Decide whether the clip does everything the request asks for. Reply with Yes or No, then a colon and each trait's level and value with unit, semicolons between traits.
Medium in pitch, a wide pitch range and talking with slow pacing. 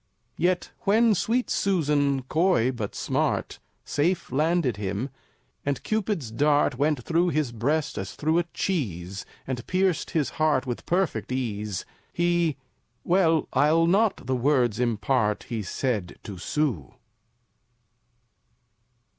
Yes: medium, 145 Hz; wide, 6.4 semitones; slow, 120 wpm